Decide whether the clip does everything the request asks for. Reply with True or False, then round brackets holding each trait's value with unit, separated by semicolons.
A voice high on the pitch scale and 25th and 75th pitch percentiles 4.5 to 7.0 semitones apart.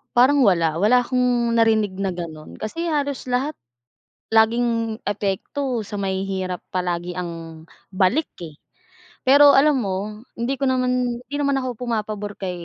True (220 Hz; 5.1 semitones)